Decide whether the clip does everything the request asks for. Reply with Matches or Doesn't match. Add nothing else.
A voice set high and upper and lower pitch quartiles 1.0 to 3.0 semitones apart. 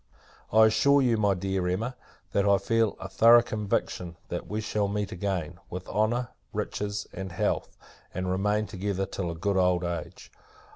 Doesn't match